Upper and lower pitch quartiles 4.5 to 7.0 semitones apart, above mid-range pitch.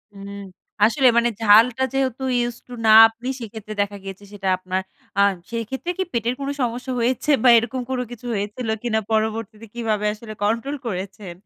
No: average, 2.9 semitones; high, 225 Hz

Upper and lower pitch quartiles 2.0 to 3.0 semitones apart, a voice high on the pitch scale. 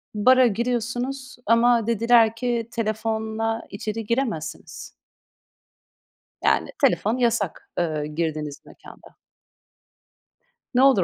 Yes: narrow, 2.6 semitones; high, 225 Hz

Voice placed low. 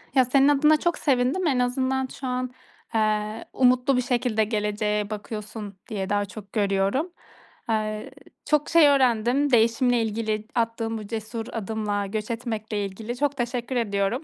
No: high, 230 Hz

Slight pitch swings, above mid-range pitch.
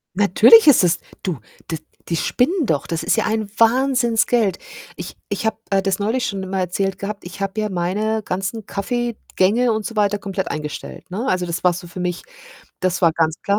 No: average, 3.6 semitones; high, 200 Hz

